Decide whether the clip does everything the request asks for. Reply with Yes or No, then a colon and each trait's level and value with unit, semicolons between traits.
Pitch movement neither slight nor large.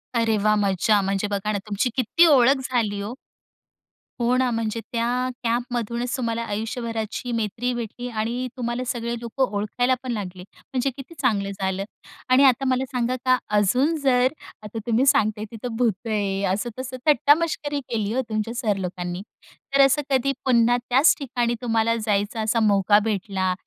Yes: average, 3.1 semitones